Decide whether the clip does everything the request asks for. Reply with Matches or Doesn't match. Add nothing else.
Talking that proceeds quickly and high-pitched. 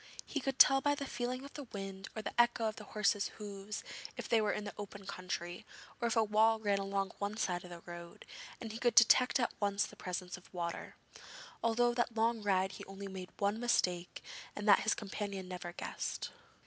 Matches